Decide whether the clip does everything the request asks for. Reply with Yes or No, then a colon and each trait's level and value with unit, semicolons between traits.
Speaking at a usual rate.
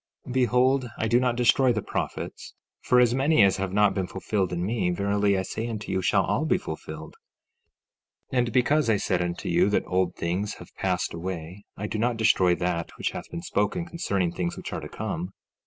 No: fast, 210 wpm